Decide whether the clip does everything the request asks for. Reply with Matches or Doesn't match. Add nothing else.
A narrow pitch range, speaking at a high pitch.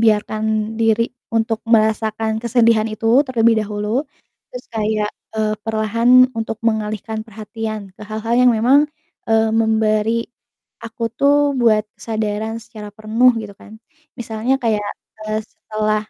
Matches